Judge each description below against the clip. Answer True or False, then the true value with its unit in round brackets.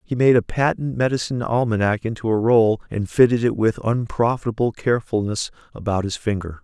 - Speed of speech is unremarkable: True (165 wpm)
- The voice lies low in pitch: True (115 Hz)